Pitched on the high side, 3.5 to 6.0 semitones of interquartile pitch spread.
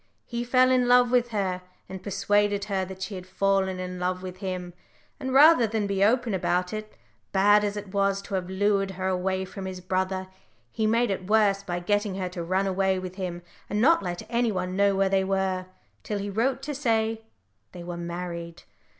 No: high, 195 Hz; narrow, 2.6 semitones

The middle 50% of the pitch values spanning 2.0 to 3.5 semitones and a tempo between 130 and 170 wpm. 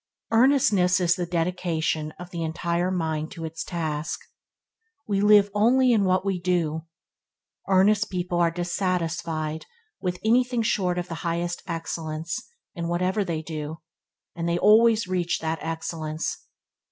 Yes: average, 2.9 semitones; average, 140 wpm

